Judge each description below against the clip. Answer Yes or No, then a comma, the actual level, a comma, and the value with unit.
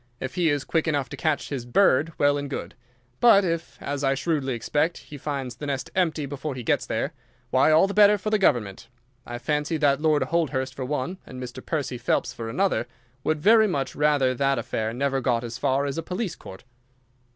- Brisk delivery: Yes, fast, 215 wpm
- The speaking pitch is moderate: Yes, medium, 145 Hz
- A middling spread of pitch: Yes, average, 3.7 semitones